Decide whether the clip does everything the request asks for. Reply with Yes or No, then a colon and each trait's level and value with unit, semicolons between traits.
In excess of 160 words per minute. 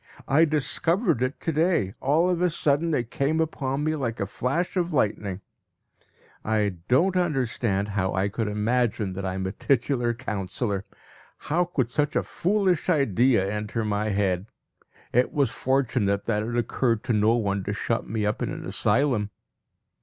Yes: average, 170 wpm